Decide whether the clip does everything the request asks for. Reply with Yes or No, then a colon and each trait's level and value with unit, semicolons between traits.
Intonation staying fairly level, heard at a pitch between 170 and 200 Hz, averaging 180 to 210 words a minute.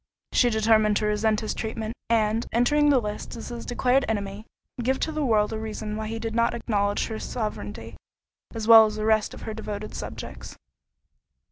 No: narrow, 1.6 semitones; high, 220 Hz; average, 190 wpm